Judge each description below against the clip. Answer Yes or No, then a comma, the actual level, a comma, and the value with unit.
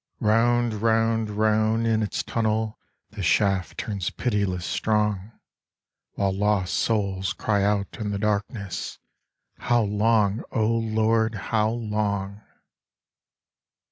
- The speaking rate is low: Yes, slow, 110 wpm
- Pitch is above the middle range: No, low, 105 Hz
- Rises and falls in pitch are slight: Yes, narrow, 1.8 semitones